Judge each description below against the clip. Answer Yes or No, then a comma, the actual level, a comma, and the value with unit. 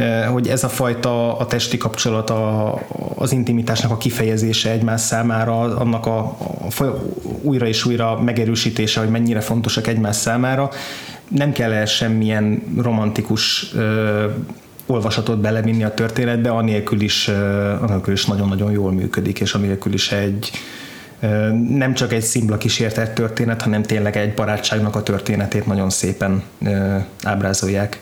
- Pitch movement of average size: No, narrow, 1.8 semitones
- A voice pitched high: No, low, 110 Hz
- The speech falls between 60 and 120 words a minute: No, average, 140 wpm